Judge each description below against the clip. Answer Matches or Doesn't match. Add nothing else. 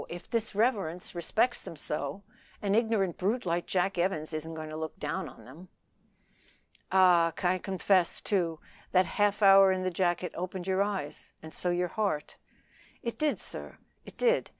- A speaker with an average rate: Matches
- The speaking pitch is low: Doesn't match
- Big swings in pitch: Doesn't match